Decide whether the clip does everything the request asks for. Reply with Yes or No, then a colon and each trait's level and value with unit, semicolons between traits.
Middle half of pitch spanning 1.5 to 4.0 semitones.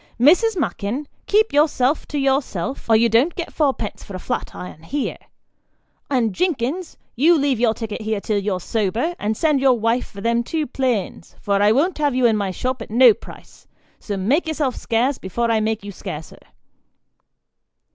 No: average, 5.2 semitones